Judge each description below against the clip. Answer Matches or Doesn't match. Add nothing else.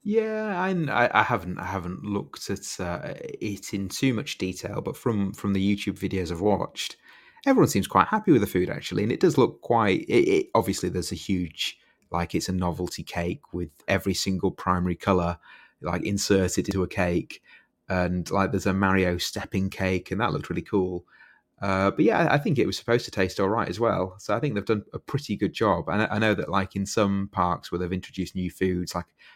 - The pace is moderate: Doesn't match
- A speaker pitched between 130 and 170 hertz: Doesn't match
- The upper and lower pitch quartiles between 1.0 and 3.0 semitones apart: Matches